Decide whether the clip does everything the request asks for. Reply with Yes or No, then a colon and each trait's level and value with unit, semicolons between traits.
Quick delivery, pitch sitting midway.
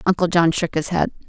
Yes: fast, 235 wpm; medium, 170 Hz